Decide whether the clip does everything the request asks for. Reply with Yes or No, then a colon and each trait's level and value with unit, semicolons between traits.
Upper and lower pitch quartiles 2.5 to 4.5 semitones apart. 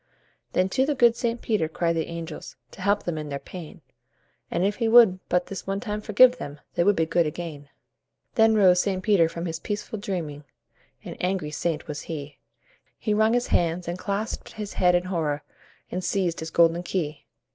Yes: average, 4.1 semitones